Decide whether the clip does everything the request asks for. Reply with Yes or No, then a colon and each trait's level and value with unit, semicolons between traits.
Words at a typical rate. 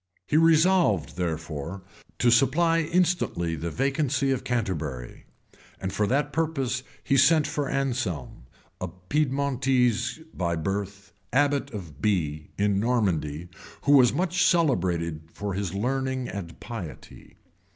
No: slow, 125 wpm